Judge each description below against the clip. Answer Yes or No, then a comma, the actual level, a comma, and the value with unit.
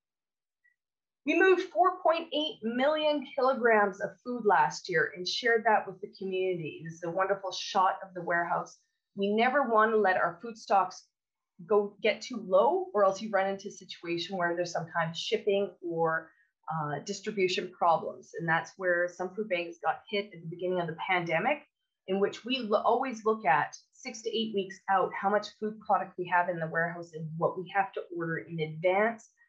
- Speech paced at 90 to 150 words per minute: No, average, 195 wpm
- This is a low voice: No, high, 195 Hz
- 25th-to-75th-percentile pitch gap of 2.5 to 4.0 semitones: No, average, 4.4 semitones